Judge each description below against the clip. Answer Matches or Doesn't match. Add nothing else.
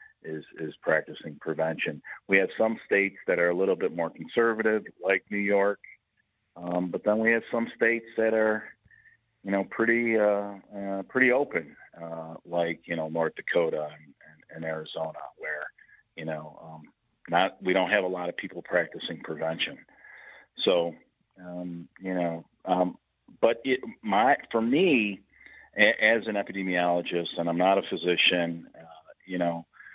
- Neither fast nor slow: Matches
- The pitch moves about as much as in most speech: Matches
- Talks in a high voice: Doesn't match